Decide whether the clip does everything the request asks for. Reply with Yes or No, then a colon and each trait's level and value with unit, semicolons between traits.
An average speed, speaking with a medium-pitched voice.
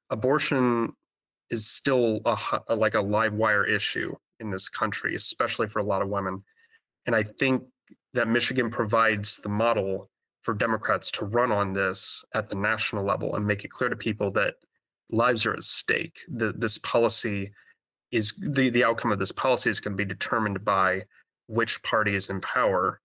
No: average, 180 wpm; low, 115 Hz